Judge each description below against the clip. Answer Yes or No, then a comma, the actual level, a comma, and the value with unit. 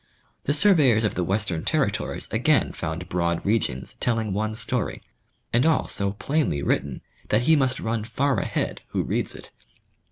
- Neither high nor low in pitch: No, low, 110 Hz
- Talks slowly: No, average, 160 wpm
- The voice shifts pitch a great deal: Yes, wide, 6.0 semitones